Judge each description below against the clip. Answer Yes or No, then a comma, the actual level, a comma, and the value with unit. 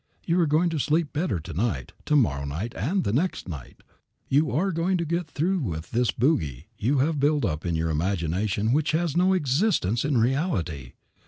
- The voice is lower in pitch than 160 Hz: Yes, low, 135 Hz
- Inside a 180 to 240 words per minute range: Yes, average, 195 wpm